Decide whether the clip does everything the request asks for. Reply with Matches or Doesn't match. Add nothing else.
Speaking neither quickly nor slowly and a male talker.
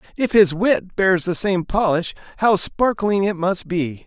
Matches